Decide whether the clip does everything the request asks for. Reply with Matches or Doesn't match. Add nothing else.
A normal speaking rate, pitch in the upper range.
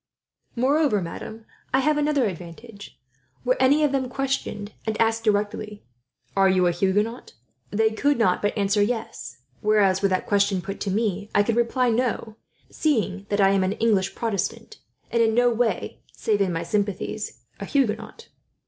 Matches